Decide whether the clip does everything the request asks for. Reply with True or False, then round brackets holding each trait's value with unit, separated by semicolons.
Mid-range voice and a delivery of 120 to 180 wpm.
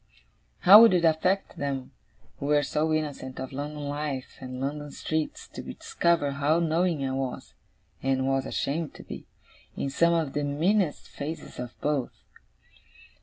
True (145 Hz; 155 wpm)